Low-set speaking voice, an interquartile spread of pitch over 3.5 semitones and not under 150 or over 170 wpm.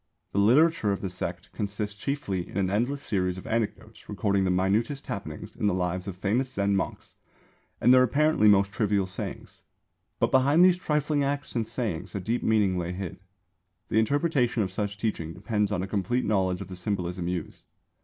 No: low, 105 Hz; average, 4.6 semitones; average, 185 wpm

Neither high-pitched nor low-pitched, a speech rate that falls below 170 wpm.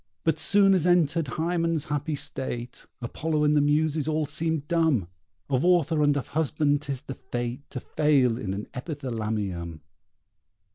Yes: medium, 145 Hz; average, 150 wpm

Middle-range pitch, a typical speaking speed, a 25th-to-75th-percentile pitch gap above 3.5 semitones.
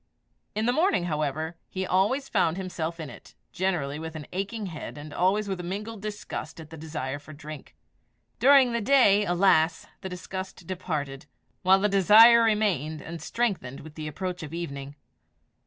Yes: medium, 180 Hz; average, 170 wpm; average, 4.8 semitones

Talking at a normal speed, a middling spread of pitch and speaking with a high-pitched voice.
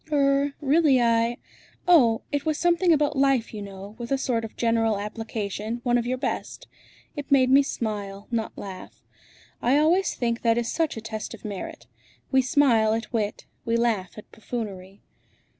Yes: average, 175 wpm; average, 4.1 semitones; high, 235 Hz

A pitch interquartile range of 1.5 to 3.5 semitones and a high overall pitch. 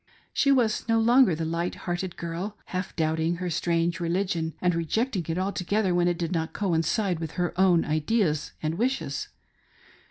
No: average, 3.2 semitones; medium, 175 Hz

